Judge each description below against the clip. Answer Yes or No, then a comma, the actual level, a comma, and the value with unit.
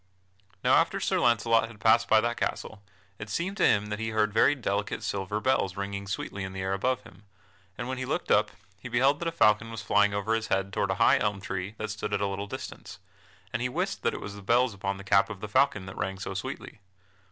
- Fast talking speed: Yes, fast, 245 wpm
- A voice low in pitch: Yes, low, 105 Hz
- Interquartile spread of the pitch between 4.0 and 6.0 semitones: No, average, 2.9 semitones